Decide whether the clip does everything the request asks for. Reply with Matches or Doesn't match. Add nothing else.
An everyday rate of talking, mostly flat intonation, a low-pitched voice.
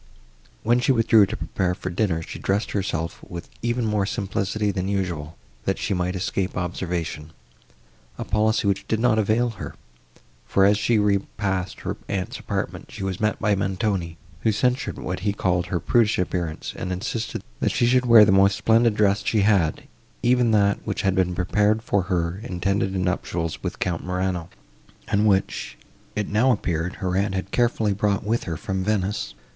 Doesn't match